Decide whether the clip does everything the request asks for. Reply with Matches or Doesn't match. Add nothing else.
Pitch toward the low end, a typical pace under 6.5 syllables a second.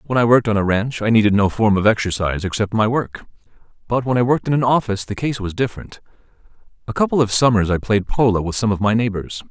Doesn't match